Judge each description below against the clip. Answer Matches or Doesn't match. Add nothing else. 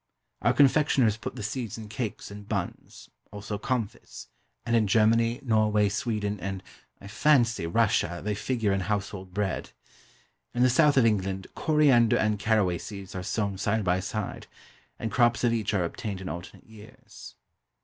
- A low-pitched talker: Matches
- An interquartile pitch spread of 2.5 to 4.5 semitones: Matches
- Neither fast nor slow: Matches